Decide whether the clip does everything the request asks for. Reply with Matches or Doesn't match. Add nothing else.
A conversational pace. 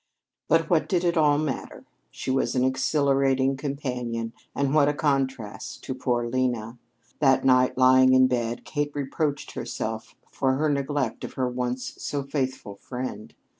Matches